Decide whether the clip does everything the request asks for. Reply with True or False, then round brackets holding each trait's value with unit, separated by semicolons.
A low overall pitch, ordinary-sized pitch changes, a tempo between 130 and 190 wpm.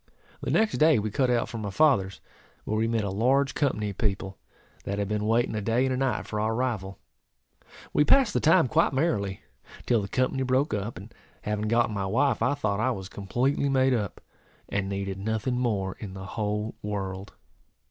False (110 Hz; 4.4 semitones; 200 wpm)